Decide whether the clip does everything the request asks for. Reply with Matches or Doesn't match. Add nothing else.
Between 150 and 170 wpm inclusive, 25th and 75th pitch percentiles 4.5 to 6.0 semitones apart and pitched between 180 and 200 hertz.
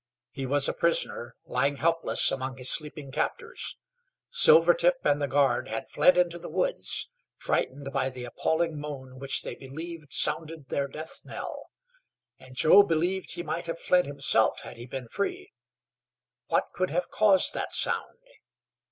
Doesn't match